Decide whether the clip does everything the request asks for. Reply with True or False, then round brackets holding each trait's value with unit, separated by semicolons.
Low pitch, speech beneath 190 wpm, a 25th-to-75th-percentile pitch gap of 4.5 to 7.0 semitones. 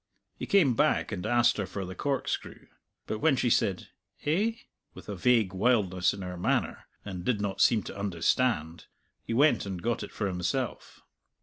True (105 Hz; 180 wpm; 5.2 semitones)